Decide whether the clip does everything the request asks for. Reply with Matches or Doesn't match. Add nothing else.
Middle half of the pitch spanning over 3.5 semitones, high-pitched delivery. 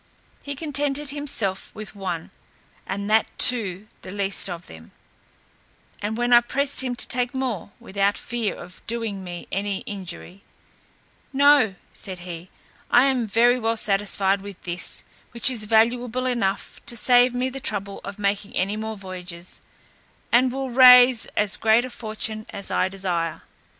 Matches